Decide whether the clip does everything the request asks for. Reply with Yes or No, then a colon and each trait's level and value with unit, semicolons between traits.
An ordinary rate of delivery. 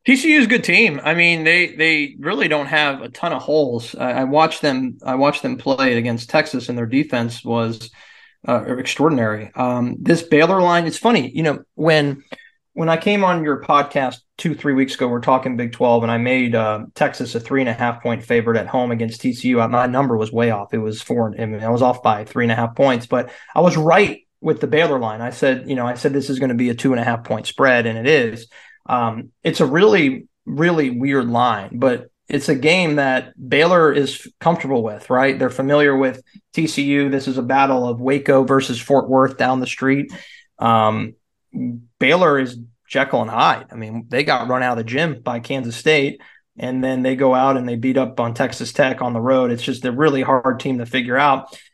No: fast, 225 wpm